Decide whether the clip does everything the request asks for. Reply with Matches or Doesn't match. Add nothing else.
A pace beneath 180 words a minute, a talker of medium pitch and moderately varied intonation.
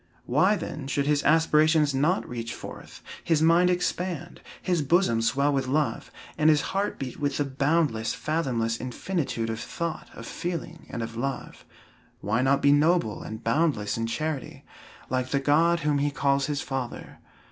Matches